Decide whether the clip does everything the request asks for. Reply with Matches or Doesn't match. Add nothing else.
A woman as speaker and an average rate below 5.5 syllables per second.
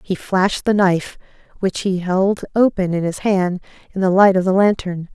Matches